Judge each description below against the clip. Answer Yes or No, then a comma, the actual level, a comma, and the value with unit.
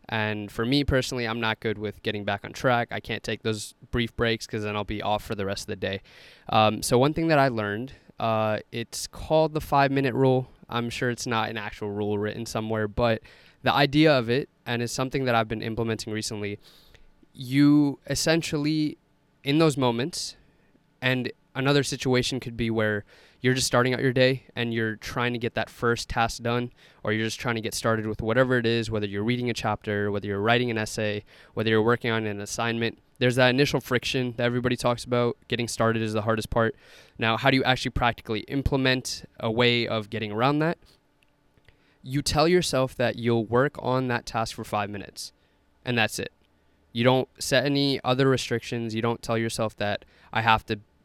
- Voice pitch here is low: Yes, low, 120 Hz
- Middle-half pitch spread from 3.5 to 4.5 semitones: No, average, 2.8 semitones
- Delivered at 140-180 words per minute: No, fast, 205 wpm